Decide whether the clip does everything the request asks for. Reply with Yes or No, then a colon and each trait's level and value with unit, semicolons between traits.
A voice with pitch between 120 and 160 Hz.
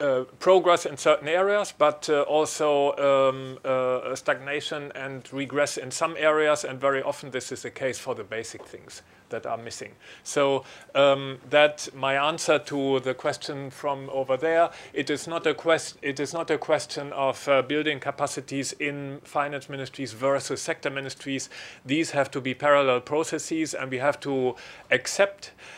Yes: medium, 140 Hz